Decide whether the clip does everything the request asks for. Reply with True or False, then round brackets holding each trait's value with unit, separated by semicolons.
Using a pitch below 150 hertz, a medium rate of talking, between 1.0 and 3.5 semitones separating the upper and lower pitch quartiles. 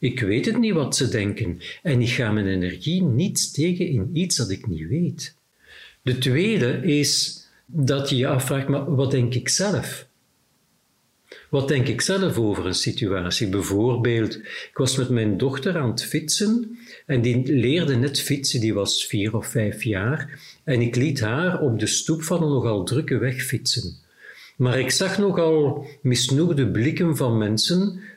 False (135 Hz; 170 wpm; 5.0 semitones)